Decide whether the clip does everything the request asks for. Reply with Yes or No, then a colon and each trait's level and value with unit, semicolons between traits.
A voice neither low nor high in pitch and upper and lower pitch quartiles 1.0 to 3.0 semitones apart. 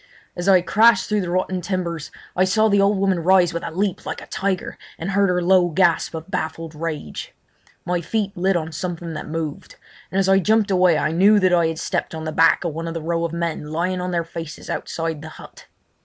Yes: medium, 175 Hz; narrow, 2.6 semitones